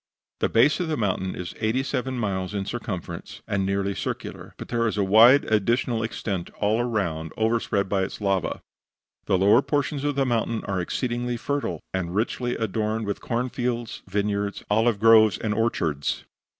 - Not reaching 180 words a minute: Yes, average, 170 wpm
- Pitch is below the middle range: Yes, low, 110 Hz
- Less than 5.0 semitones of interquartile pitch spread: Yes, average, 3.5 semitones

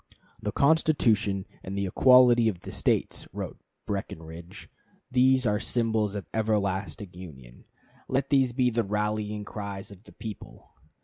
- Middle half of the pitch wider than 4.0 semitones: No, average, 3.6 semitones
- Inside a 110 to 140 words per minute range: Yes, slow, 135 wpm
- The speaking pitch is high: No, low, 105 Hz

